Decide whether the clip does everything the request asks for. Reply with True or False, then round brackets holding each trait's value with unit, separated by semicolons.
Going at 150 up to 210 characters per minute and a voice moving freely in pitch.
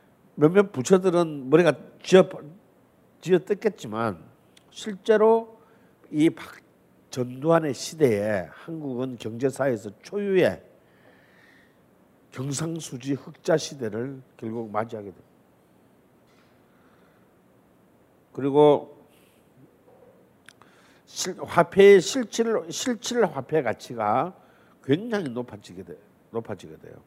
True (195 characters per minute; 7.5 semitones)